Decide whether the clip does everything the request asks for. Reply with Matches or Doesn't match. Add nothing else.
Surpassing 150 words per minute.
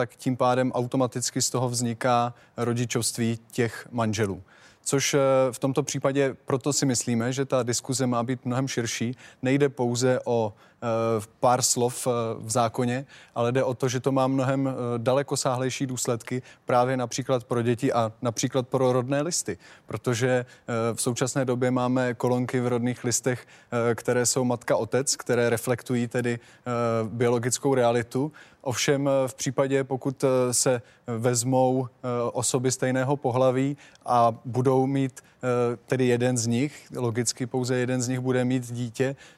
Doesn't match